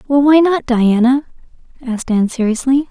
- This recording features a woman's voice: Yes, female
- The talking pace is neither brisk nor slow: Yes, average, 145 wpm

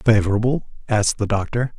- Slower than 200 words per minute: Yes, slow, 135 wpm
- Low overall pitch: Yes, low, 110 Hz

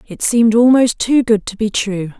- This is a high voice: Yes, high, 220 Hz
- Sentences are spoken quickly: Yes, fast, 220 wpm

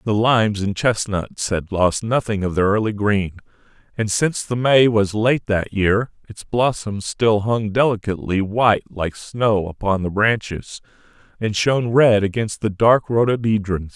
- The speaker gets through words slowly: No, average, 160 wpm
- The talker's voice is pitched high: No, low, 105 Hz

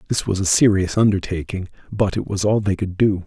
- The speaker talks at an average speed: No, fast, 220 wpm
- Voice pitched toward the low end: Yes, low, 100 Hz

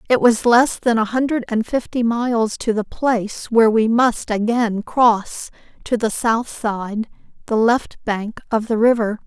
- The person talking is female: Yes, female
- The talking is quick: No, average, 175 wpm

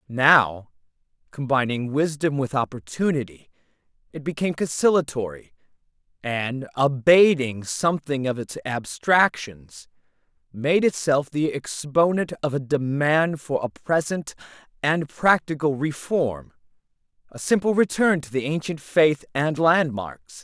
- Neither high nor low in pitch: Yes, medium, 145 Hz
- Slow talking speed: Yes, slow, 105 wpm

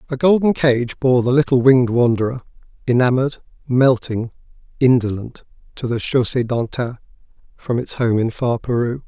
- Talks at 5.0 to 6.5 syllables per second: Yes, 5.1 syllables/s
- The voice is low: Yes, low, 125 Hz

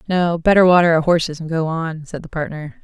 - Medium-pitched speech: Yes, medium, 165 Hz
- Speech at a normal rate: No, fast, 235 wpm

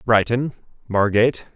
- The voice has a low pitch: Yes, low, 115 Hz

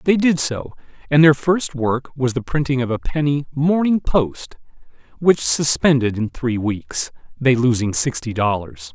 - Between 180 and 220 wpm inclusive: No, average, 160 wpm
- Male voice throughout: Yes, male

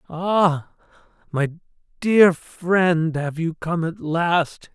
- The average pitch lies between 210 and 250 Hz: No, medium, 170 Hz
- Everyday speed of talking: No, slow, 115 wpm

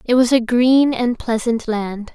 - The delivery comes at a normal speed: Yes, average, 195 wpm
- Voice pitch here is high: Yes, high, 235 Hz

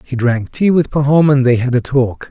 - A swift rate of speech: Yes, fast, 260 wpm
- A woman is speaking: No, male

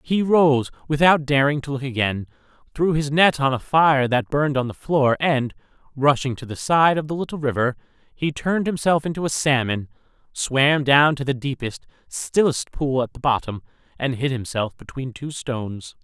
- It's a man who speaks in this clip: Yes, male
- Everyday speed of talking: Yes, average, 185 wpm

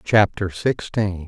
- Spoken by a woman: No, male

